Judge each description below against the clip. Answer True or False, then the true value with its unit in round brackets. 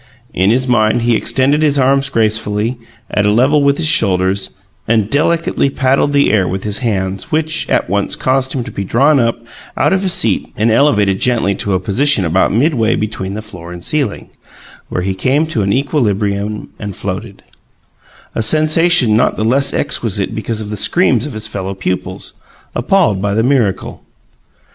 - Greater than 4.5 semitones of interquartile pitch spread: True (5.6 semitones)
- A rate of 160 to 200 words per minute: True (180 wpm)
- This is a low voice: True (110 Hz)